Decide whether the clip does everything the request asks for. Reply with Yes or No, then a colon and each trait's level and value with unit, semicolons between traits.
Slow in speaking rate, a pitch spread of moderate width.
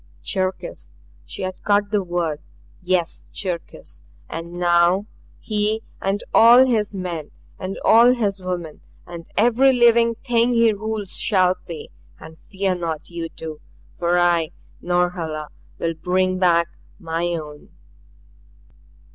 Yes: slow, 125 wpm; average, 3.6 semitones